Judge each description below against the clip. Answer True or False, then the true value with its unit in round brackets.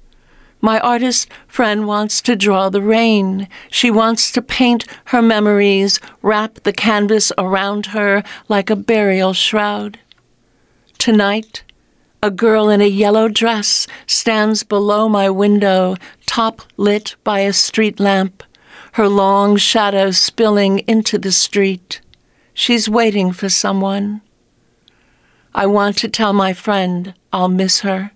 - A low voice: False (205 Hz)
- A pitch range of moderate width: False (1.9 semitones)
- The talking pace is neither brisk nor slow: False (130 wpm)